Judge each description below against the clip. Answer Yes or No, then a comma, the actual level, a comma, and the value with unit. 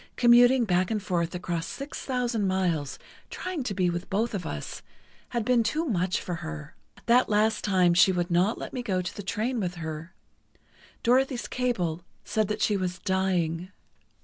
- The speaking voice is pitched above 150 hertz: Yes, high, 190 Hz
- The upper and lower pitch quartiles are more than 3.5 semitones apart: Yes, average, 5.1 semitones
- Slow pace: No, average, 175 wpm